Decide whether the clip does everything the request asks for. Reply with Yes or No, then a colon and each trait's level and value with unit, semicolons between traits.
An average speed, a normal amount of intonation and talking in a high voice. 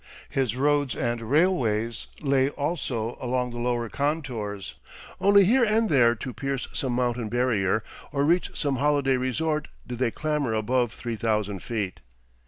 No: average, 145 wpm; average, 3.9 semitones; low, 125 Hz